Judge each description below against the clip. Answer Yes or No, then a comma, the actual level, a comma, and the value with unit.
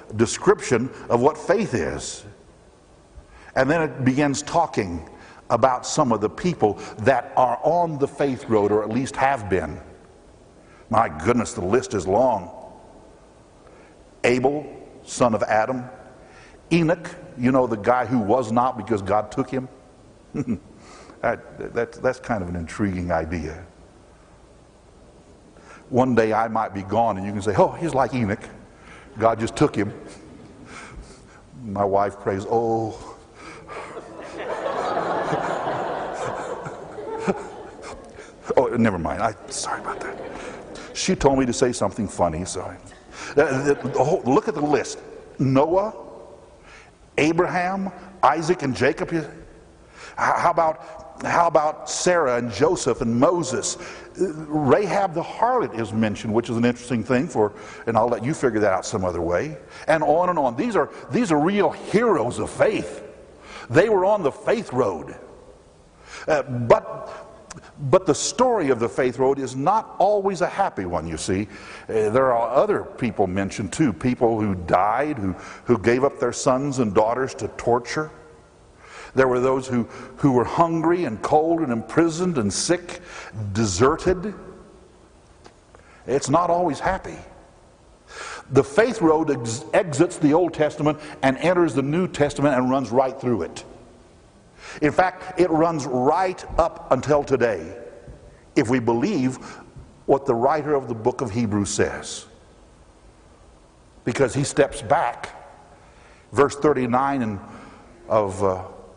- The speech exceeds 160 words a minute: No, average, 140 wpm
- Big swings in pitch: Yes, wide, 6.3 semitones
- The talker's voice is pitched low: Yes, low, 130 Hz